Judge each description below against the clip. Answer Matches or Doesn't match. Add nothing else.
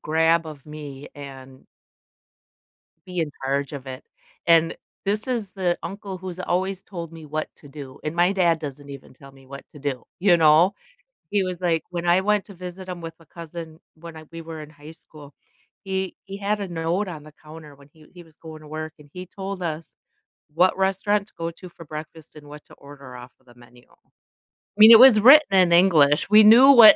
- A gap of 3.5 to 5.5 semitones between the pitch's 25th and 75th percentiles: Matches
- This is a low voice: Doesn't match